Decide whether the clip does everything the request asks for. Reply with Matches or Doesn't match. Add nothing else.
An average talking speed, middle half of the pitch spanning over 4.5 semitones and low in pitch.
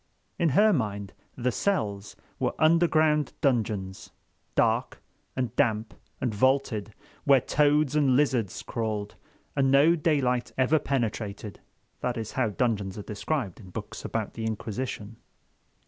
Doesn't match